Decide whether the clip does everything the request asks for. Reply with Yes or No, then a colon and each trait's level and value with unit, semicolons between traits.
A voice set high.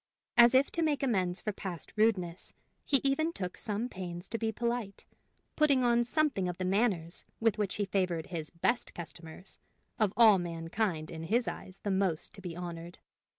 Yes: high, 195 Hz